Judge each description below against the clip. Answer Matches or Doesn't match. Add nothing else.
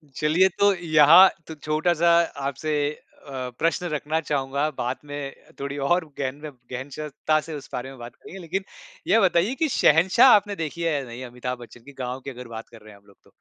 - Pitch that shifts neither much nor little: Matches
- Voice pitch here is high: Doesn't match